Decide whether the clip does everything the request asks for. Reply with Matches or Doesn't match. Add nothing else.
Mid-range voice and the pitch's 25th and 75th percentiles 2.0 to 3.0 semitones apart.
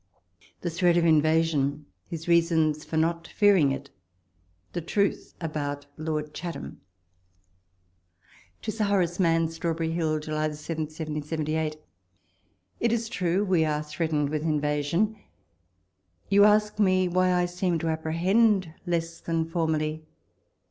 Matches